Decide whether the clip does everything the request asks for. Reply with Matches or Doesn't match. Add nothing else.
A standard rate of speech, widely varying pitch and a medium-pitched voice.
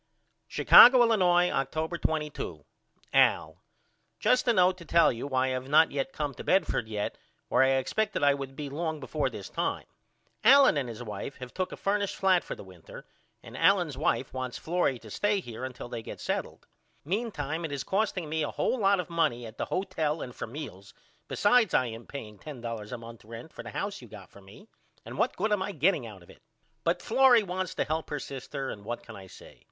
Doesn't match